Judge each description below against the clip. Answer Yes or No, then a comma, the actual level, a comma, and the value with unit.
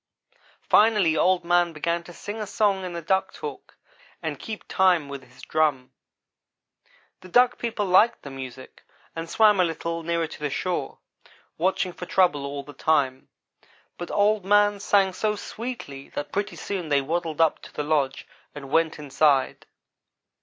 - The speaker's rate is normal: Yes, average, 165 wpm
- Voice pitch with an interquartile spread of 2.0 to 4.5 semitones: No, average, 5.0 semitones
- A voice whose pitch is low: No, medium, 170 Hz